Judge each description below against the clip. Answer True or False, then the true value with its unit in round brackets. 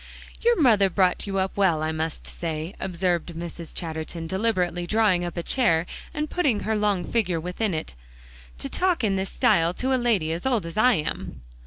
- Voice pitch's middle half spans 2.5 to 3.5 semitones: False (4.8 semitones)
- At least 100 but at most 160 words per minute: False (190 wpm)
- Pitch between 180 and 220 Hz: True (185 Hz)